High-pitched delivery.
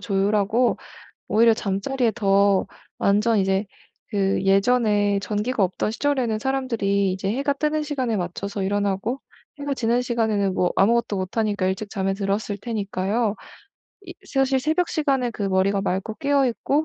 Yes: high, 215 Hz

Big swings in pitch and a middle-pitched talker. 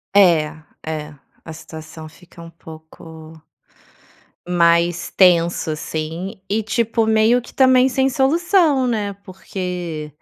Yes: wide, 6.2 semitones; medium, 180 Hz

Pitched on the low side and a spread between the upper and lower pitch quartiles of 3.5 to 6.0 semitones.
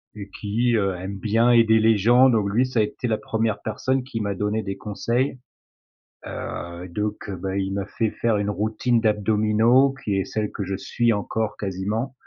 No: low, 110 Hz; narrow, 2.6 semitones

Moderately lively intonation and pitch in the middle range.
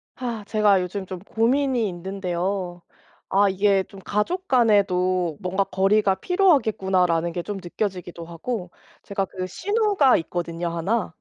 No: average, 3.5 semitones; high, 195 Hz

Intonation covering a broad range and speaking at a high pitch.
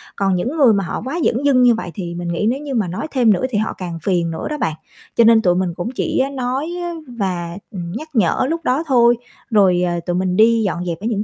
Yes: wide, 5.9 semitones; high, 210 Hz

